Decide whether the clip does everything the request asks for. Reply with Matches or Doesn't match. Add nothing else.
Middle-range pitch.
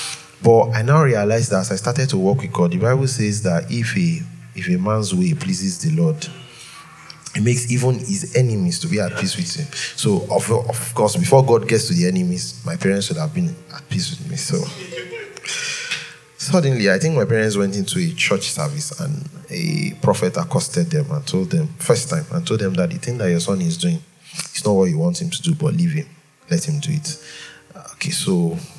Matches